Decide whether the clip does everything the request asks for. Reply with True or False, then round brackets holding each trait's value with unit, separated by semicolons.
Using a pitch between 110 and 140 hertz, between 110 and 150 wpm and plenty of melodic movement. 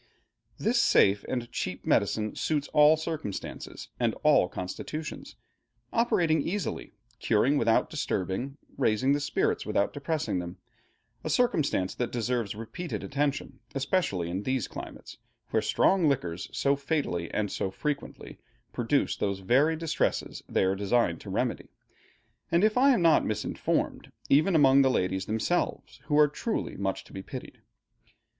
True (135 Hz; 140 wpm; 7.7 semitones)